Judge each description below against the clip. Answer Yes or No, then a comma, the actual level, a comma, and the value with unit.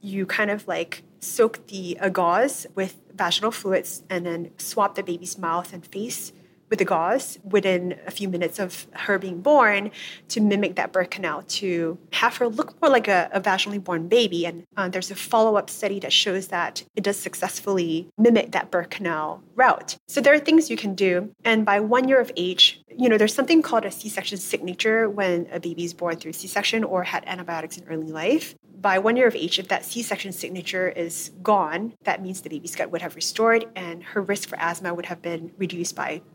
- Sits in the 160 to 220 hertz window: Yes, high, 190 Hz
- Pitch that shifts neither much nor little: Yes, average, 3.2 semitones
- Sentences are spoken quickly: Yes, fast, 215 wpm